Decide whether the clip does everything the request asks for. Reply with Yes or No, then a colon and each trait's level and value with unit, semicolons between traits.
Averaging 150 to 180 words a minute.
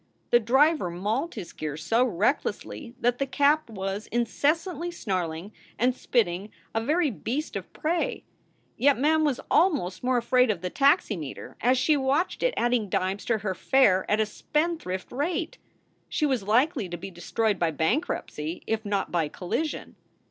Yes: average, 160 wpm